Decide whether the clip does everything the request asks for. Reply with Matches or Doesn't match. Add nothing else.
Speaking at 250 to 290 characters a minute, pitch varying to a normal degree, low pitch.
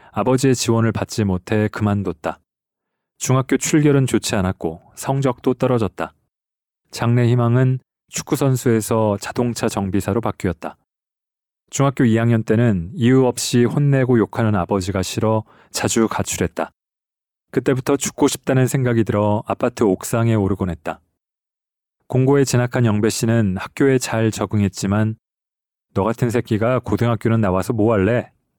Doesn't match